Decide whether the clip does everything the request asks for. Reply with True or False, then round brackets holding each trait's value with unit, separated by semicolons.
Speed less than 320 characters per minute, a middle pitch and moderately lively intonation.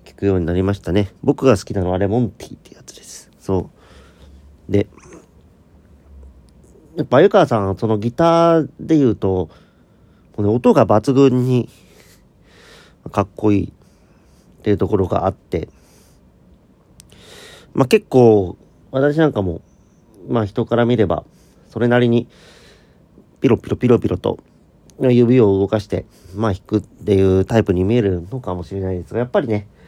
False (280 characters per minute; 105 Hz; 4.8 semitones)